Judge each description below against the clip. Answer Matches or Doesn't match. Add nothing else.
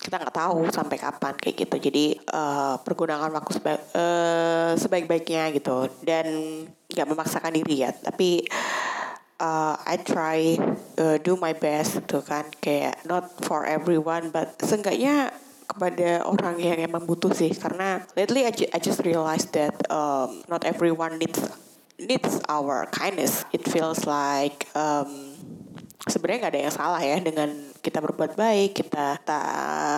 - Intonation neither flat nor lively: Doesn't match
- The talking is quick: Matches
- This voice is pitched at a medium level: Matches